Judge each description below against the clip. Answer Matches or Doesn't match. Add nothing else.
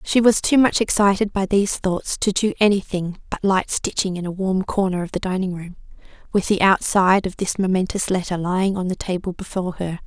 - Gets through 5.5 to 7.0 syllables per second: Matches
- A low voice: Doesn't match